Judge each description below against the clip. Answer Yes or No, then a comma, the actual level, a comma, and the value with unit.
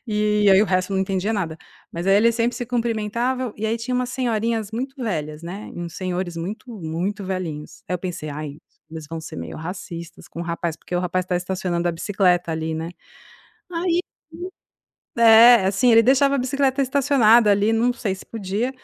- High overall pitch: Yes, high, 200 Hz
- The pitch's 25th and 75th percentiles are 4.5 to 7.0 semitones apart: Yes, average, 5.1 semitones